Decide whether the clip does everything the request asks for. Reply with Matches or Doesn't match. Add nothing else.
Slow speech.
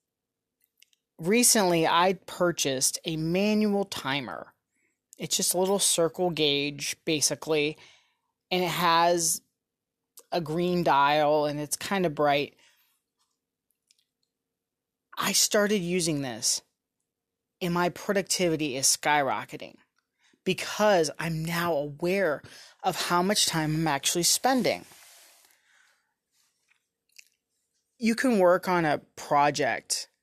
Matches